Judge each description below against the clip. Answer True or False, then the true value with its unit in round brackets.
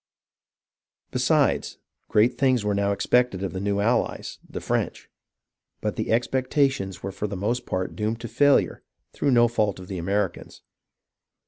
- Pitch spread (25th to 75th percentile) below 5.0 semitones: True (3.9 semitones)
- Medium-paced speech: True (150 wpm)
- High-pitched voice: False (105 Hz)